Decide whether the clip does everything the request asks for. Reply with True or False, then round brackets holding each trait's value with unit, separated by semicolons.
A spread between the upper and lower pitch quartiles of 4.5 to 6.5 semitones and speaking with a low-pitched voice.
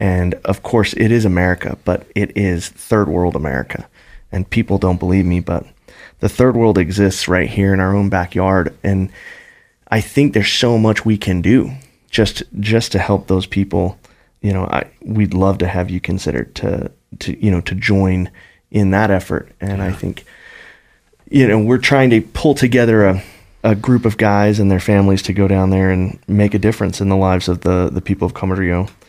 False (2.6 semitones; 100 Hz)